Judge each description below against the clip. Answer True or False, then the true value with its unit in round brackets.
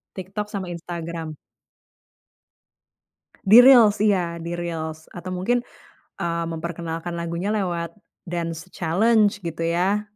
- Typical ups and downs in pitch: True (3.0 semitones)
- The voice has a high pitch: False (175 Hz)